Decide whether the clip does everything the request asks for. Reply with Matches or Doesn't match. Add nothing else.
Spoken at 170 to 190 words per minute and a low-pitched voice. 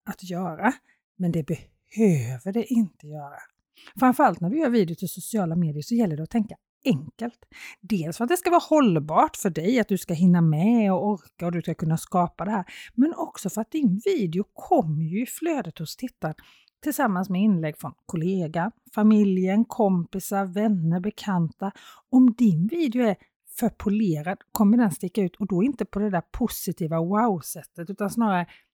Doesn't match